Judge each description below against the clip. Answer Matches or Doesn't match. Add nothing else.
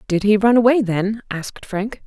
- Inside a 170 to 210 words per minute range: Matches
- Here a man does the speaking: Doesn't match